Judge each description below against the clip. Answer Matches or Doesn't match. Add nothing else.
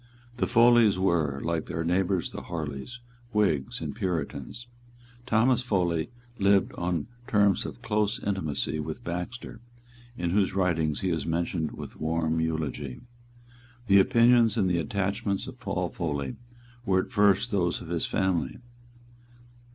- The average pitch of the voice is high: Doesn't match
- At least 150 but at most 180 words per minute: Doesn't match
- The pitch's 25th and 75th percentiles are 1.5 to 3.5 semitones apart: Doesn't match